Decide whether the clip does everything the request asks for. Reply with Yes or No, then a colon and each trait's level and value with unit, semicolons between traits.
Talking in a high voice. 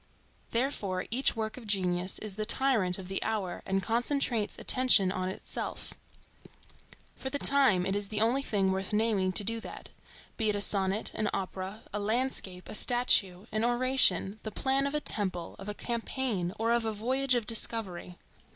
Yes: high, 215 Hz